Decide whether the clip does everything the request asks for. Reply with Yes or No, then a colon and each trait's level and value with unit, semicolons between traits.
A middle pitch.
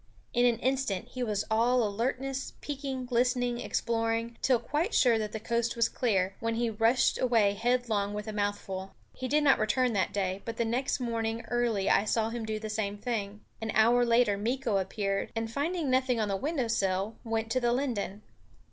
No: high, 230 Hz